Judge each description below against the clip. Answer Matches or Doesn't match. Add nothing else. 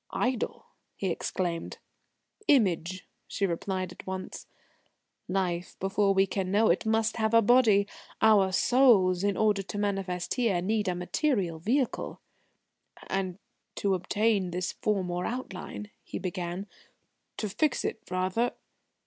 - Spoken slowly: Matches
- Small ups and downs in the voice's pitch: Doesn't match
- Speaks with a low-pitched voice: Doesn't match